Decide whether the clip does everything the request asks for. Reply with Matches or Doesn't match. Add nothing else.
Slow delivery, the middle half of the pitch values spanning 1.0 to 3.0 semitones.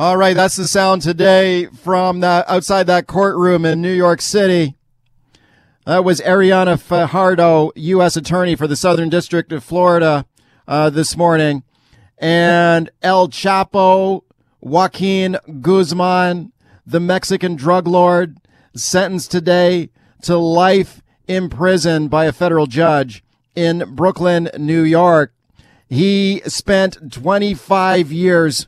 Matches